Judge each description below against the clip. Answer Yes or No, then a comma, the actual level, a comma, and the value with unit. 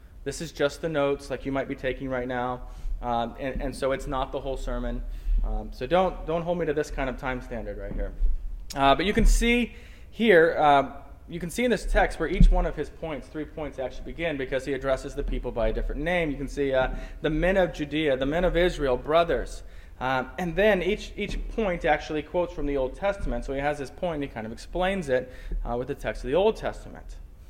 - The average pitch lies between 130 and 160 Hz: Yes, medium, 140 Hz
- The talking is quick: Yes, fast, 240 wpm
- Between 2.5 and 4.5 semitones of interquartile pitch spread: No, average, 5.3 semitones